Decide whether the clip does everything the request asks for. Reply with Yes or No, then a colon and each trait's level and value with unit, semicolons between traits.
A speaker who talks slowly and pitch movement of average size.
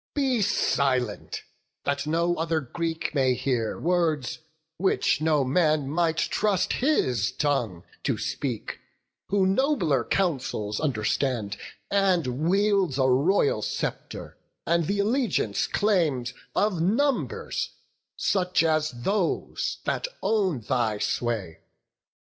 No: slow, 105 wpm; wide, 6.9 semitones